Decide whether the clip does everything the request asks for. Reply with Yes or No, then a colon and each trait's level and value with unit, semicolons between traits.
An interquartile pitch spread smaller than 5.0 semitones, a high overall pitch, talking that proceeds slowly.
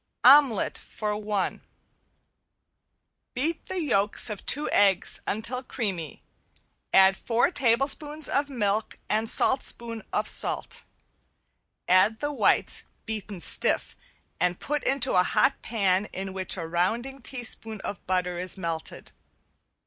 No: average, 5.3 semitones; high, 215 Hz; slow, 120 wpm